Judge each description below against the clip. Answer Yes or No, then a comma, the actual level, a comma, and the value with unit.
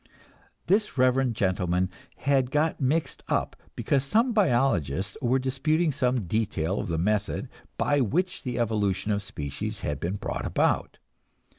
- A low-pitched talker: Yes, low, 120 Hz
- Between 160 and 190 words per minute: No, average, 140 wpm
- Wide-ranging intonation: Yes, wide, 6.2 semitones